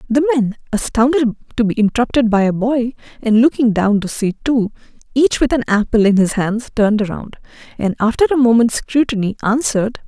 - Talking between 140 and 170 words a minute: No, average, 180 wpm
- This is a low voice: No, high, 235 Hz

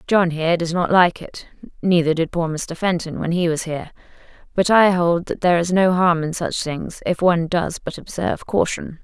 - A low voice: No, medium, 170 Hz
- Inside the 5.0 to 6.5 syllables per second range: Yes, 5.1 syllables/s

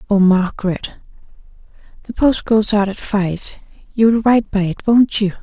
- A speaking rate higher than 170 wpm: No, average, 155 wpm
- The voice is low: No, high, 205 Hz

